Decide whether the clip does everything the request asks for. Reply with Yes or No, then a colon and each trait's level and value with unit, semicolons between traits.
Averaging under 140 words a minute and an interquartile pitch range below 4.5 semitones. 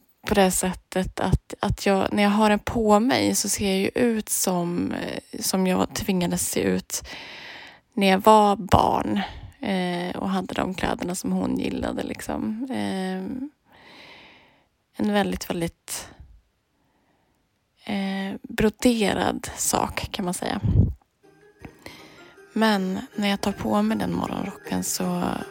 Yes: average, 130 wpm; average, 2.9 semitones